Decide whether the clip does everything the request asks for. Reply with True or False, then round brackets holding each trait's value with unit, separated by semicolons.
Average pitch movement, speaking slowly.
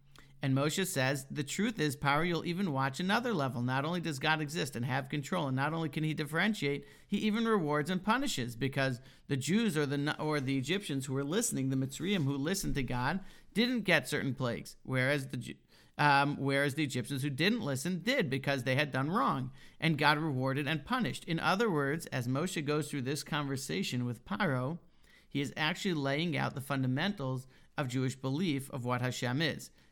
False (3.7 semitones; 195 wpm)